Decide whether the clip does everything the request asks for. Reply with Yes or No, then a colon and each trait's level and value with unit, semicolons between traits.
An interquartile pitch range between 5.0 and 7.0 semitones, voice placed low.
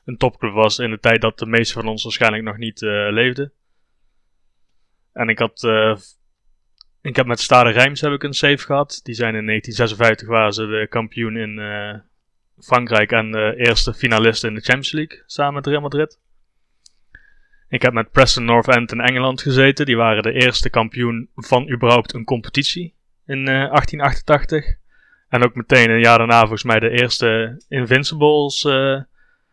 No: average, 3.4 semitones; low, 120 Hz